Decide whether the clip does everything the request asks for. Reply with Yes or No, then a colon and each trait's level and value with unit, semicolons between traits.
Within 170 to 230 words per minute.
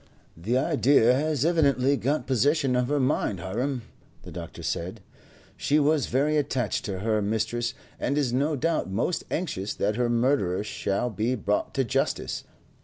No: average, 160 wpm